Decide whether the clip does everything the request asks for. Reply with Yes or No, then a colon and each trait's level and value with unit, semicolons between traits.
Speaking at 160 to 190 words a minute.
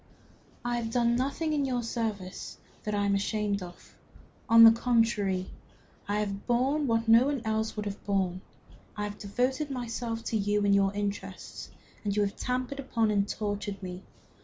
Yes: average, 175 wpm